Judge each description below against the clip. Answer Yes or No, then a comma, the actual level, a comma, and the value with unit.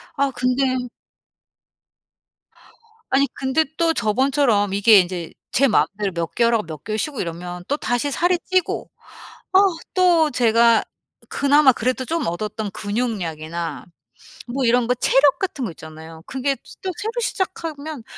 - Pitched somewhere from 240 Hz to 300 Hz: Yes, high, 245 Hz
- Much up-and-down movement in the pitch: Yes, wide, 5.8 semitones